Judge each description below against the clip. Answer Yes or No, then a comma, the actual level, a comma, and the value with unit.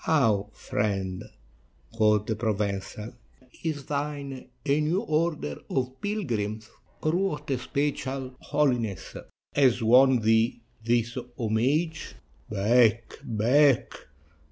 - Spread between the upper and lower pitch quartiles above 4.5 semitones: Yes, average, 5.0 semitones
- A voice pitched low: Yes, low, 125 Hz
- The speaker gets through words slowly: Yes, slow, 95 wpm